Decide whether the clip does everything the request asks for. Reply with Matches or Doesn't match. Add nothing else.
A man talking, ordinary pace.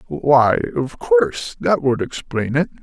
Matches